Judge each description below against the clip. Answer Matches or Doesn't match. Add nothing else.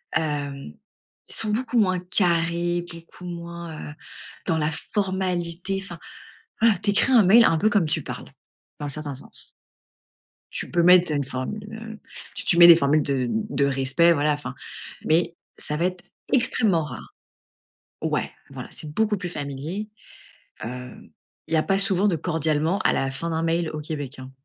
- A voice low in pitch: Doesn't match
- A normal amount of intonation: Matches